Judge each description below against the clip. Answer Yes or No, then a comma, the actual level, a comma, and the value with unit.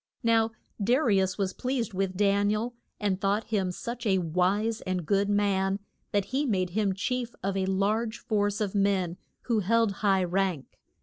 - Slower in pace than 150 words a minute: No, average, 185 wpm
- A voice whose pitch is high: Yes, high, 200 Hz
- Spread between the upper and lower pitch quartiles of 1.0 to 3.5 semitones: Yes, average, 2.7 semitones